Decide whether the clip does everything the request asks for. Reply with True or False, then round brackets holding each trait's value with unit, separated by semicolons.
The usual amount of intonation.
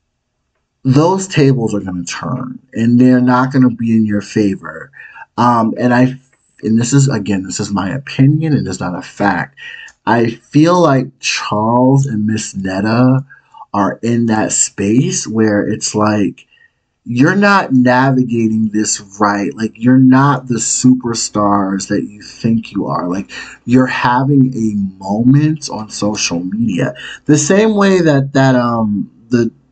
True (3.8 semitones)